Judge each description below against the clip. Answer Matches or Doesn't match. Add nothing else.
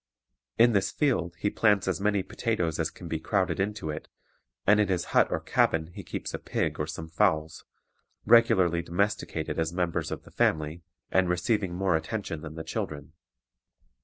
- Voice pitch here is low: Matches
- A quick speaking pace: Doesn't match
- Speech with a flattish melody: Doesn't match